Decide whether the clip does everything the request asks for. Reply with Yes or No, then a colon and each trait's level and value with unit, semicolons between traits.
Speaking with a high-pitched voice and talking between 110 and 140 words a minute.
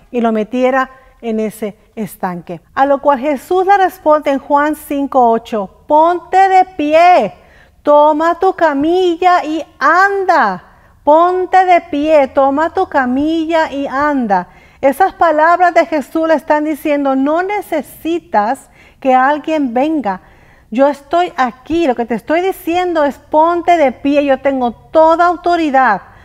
Yes: very high, 300 Hz; average, 135 wpm